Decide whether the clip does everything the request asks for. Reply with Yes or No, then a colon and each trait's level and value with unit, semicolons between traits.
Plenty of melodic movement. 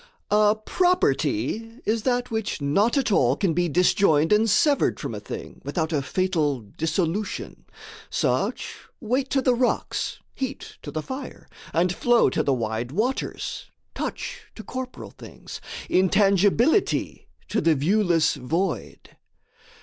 Yes: wide, 6.8 semitones